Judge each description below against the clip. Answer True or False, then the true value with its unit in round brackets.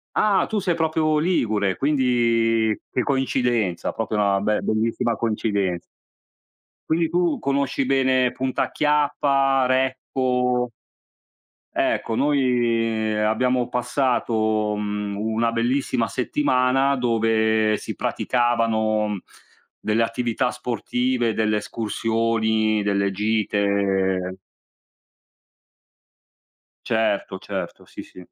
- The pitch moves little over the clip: False (3.2 semitones)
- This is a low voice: True (115 Hz)